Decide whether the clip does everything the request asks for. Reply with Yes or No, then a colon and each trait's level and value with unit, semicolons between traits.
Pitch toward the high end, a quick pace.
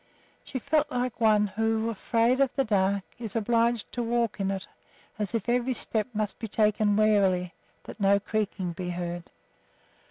No: high, 215 Hz; average, 165 wpm